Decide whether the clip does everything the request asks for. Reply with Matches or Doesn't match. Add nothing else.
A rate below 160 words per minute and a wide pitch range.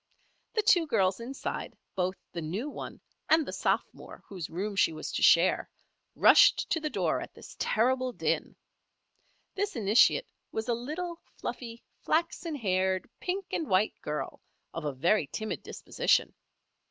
Matches